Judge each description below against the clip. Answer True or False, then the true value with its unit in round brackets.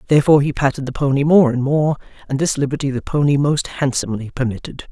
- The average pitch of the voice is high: False (140 Hz)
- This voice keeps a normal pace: True (195 wpm)